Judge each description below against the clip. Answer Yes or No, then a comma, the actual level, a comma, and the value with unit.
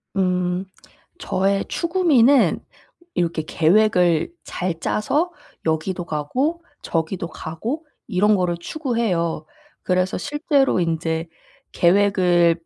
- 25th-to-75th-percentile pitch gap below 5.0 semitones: No, wide, 5.5 semitones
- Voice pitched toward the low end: No, medium, 185 Hz